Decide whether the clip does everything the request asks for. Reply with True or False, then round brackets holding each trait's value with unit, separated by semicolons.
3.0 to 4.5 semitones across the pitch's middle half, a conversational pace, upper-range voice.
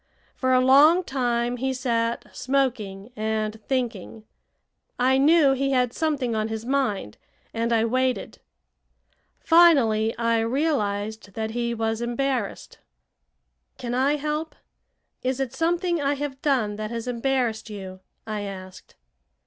False (3.6 semitones; 130 wpm; 245 Hz)